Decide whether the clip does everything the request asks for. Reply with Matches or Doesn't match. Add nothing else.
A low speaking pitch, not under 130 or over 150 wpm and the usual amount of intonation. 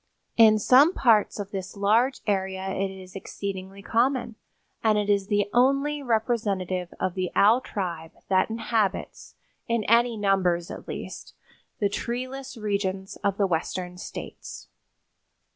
Doesn't match